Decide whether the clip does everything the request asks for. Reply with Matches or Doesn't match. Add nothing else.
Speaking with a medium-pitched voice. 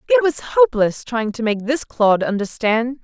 Doesn't match